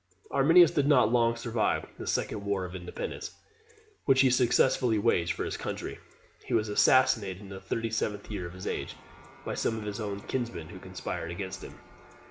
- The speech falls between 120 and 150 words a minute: No, average, 185 wpm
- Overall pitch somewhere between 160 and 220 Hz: No, low, 110 Hz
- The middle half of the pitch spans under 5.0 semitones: Yes, average, 4.3 semitones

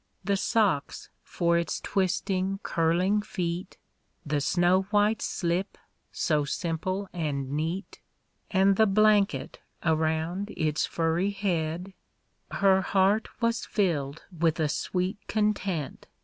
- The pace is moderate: No, slow, 115 wpm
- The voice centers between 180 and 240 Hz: Yes, medium, 185 Hz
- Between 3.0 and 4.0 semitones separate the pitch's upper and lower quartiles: Yes, average, 3.5 semitones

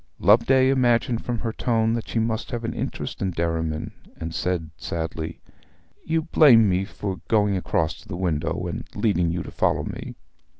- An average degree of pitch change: No, wide, 5.7 semitones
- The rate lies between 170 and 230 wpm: Yes, average, 175 wpm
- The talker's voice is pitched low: Yes, low, 100 Hz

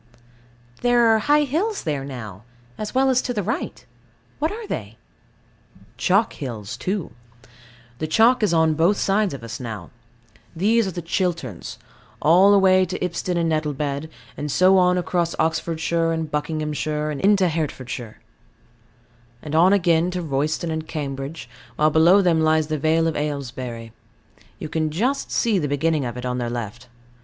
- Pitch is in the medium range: Yes, medium, 160 Hz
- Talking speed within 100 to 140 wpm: No, average, 160 wpm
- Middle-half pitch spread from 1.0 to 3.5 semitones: No, average, 4.6 semitones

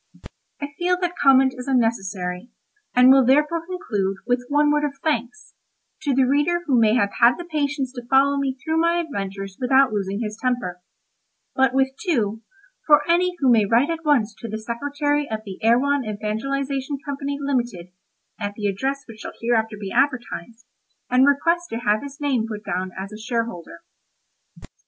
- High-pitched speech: Yes, very high, 255 Hz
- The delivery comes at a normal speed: Yes, average, 175 wpm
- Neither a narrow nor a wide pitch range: Yes, average, 4.6 semitones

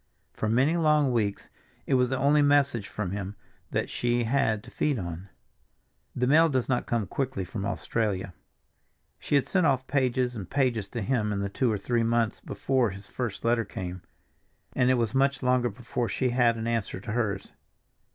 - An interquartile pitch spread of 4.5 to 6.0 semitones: No, average, 4.1 semitones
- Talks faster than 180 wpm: Yes, average, 190 wpm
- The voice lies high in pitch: No, low, 120 Hz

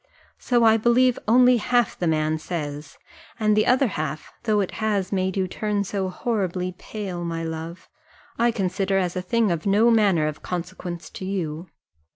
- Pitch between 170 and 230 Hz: Yes, high, 190 Hz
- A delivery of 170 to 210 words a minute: Yes, average, 175 wpm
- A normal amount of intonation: Yes, average, 4.2 semitones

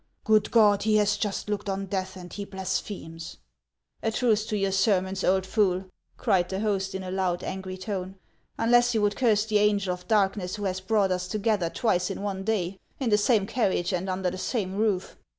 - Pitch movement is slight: Yes, narrow, 2.2 semitones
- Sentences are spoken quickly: Yes, fast, 220 wpm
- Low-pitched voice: No, high, 195 Hz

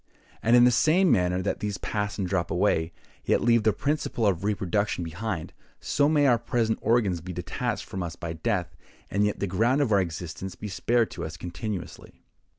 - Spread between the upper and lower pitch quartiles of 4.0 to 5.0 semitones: Yes, average, 4.6 semitones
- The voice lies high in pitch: No, low, 105 Hz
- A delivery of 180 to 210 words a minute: Yes, average, 195 wpm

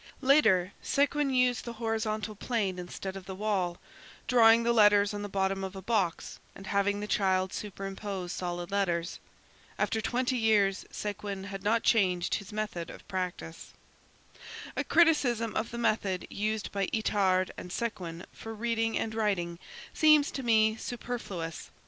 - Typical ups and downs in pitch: Yes, average, 3.1 semitones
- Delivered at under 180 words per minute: Yes, average, 150 wpm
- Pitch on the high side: Yes, high, 205 Hz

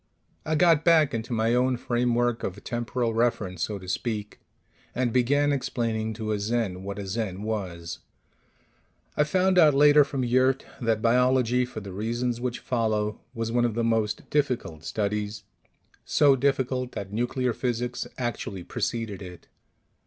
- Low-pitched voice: Yes, low, 120 Hz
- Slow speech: No, average, 155 wpm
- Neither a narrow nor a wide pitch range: Yes, average, 3.2 semitones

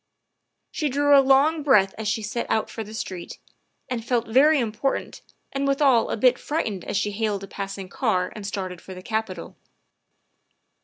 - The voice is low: No, high, 220 Hz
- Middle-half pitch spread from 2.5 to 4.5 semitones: No, average, 5.3 semitones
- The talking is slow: No, average, 190 wpm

